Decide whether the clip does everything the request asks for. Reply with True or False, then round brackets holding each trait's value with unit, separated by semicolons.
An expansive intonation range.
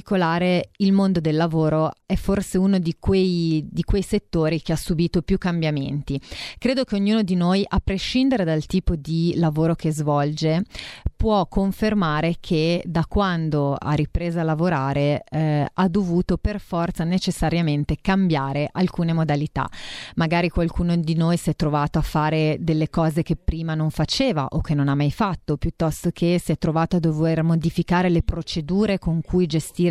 False (2.6 semitones)